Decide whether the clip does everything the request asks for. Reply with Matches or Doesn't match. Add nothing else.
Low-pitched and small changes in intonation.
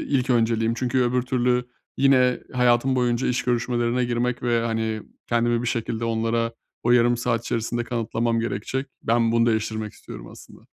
Matches